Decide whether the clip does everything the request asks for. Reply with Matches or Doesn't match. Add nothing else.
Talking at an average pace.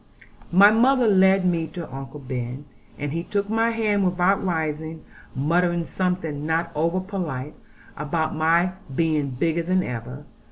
Matches